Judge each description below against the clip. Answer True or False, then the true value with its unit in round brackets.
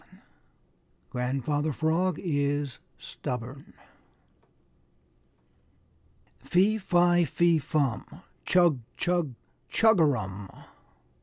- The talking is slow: True (65 wpm)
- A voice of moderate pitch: True (150 Hz)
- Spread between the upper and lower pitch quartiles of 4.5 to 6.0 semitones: True (4.8 semitones)